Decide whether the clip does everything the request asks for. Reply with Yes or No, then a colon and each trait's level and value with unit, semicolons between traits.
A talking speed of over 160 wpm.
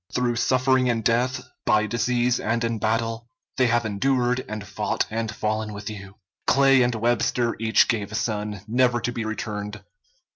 Yes: average, 170 wpm